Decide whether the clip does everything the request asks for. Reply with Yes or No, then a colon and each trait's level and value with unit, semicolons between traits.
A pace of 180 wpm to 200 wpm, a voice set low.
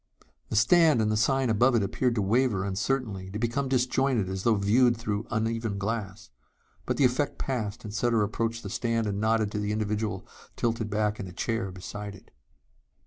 Yes: average, 190 wpm; low, 110 Hz